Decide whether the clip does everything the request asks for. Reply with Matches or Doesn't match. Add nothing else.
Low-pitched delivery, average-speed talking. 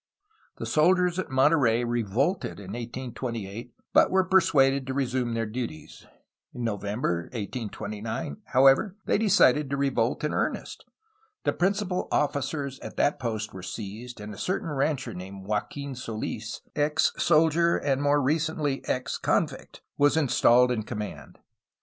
Matches